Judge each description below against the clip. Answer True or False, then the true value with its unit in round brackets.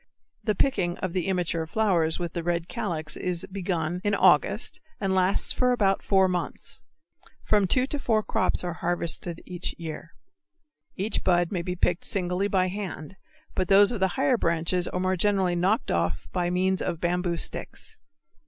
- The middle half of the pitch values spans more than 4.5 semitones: False (2.4 semitones)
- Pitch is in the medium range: True (180 Hz)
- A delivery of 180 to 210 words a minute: False (170 wpm)